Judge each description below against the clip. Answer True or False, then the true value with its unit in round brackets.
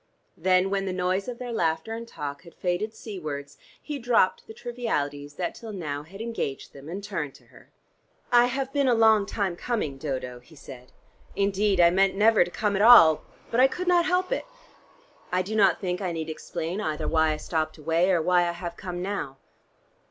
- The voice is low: False (185 Hz)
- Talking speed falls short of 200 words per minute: False (205 wpm)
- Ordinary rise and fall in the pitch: False (5.7 semitones)